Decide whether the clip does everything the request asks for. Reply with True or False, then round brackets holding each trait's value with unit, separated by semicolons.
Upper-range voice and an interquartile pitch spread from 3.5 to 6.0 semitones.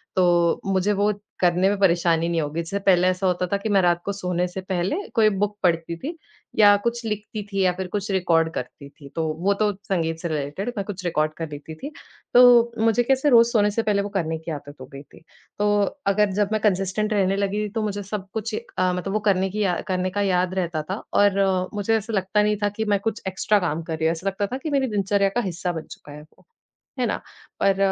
False (195 Hz; 3.1 semitones)